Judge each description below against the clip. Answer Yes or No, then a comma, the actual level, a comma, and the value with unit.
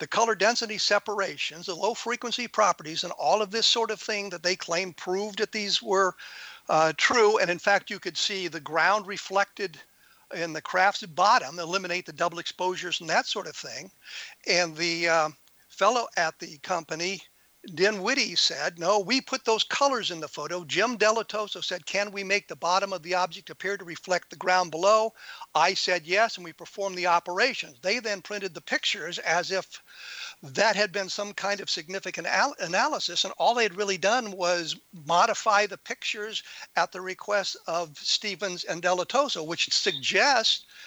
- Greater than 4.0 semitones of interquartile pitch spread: No, average, 3.3 semitones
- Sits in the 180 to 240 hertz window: Yes, high, 190 Hz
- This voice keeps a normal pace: Yes, average, 180 wpm